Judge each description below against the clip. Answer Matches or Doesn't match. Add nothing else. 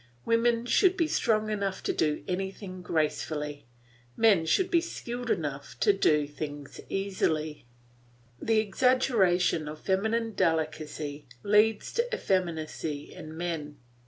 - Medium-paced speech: Doesn't match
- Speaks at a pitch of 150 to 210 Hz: Matches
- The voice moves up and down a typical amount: Doesn't match